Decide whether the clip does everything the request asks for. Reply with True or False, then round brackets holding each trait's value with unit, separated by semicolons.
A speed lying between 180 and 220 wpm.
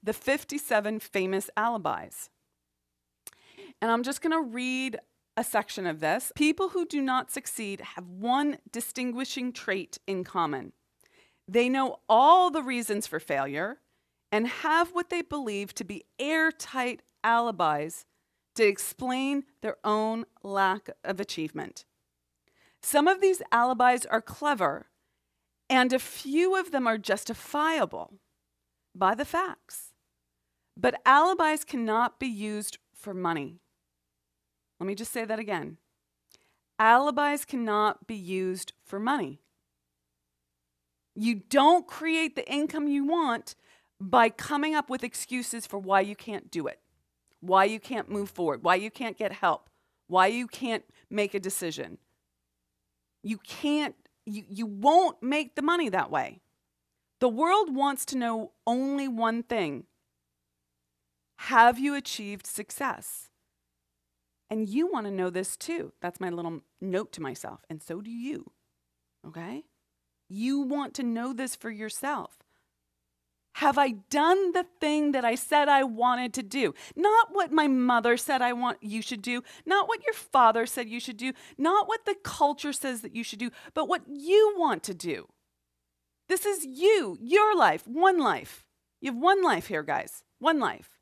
False (150 wpm)